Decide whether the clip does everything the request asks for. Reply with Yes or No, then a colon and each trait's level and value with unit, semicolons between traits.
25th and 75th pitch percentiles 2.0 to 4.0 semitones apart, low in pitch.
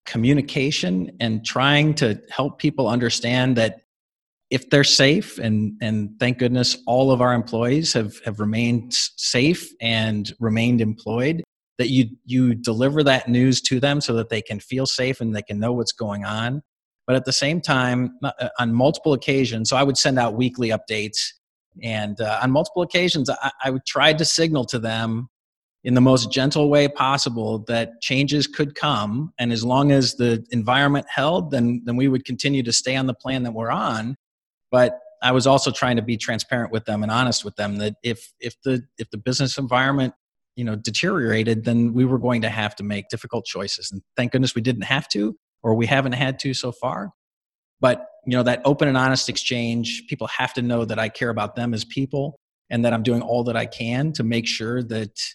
Yes: average, 2.7 semitones; low, 125 Hz